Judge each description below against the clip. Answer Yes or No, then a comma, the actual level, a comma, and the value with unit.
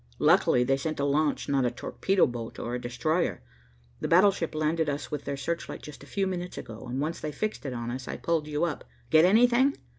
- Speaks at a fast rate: Yes, fast, 220 wpm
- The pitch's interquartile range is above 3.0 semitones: Yes, average, 4.2 semitones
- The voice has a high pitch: No, medium, 150 Hz